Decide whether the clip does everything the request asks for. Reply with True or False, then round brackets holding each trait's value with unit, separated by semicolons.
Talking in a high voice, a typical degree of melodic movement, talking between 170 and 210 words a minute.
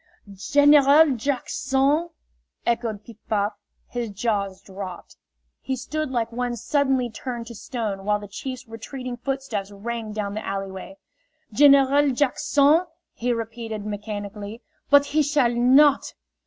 False (240 Hz; 4.7 semitones; 135 wpm)